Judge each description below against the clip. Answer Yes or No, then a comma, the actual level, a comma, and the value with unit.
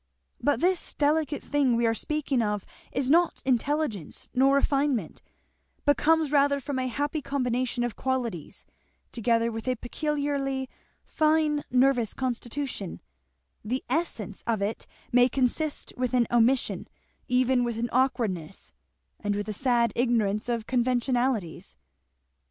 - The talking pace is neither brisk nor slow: No, slow, 130 wpm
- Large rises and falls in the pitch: No, average, 3.4 semitones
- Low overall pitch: No, very high, 255 Hz